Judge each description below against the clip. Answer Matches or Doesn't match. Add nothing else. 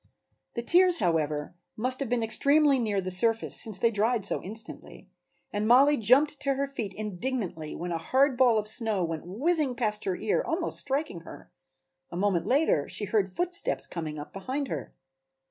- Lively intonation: Matches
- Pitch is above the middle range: Matches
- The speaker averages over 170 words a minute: Matches